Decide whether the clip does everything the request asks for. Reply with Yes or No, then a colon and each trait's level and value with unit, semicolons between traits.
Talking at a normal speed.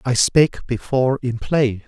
Yes: average, 160 wpm